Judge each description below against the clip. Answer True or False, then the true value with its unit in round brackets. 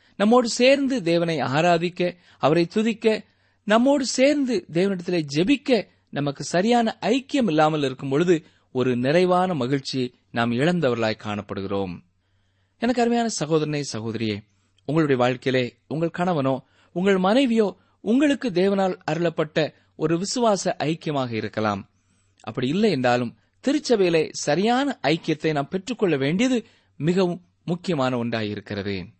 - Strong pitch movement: True (8.3 semitones)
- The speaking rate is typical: True (105 wpm)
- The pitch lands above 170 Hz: False (165 Hz)